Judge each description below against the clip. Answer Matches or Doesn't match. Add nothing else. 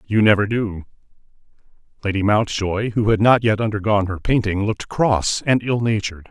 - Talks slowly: Doesn't match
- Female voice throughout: Doesn't match